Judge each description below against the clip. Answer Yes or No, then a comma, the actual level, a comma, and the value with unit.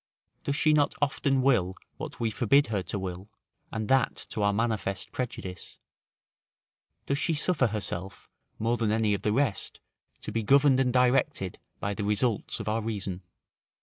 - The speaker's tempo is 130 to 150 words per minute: No, average, 165 wpm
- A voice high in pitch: No, low, 115 Hz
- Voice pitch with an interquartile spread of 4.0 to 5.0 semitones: Yes, average, 4.7 semitones